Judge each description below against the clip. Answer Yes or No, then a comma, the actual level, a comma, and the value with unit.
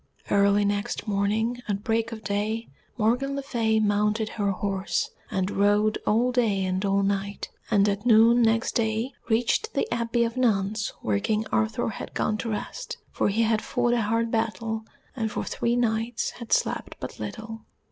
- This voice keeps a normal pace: Yes, average, 175 wpm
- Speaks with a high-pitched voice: Yes, high, 220 Hz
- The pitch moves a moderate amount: No, narrow, 2.1 semitones